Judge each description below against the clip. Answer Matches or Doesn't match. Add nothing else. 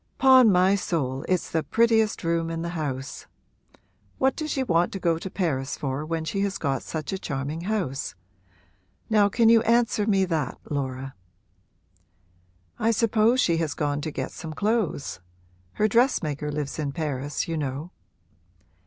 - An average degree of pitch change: Doesn't match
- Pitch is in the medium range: Matches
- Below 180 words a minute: Matches